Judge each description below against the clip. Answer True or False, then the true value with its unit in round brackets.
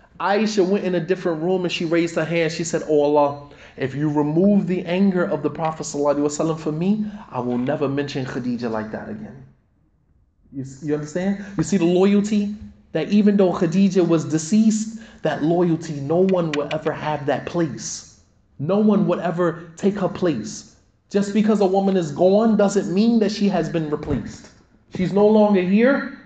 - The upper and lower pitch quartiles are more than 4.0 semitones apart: True (4.8 semitones)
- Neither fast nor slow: True (180 wpm)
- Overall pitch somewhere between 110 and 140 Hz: False (175 Hz)